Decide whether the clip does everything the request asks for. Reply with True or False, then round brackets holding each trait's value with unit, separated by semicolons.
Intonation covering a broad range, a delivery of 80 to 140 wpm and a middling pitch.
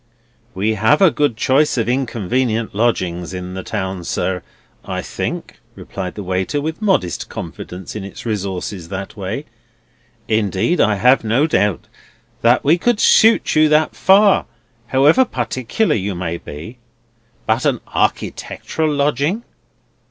False (7.7 semitones; 135 wpm; 115 Hz)